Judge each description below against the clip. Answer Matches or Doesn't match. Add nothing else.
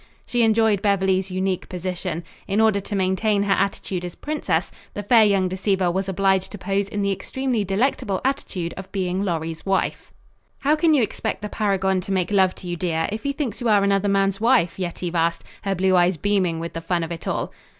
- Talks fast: Matches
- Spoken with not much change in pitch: Matches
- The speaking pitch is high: Matches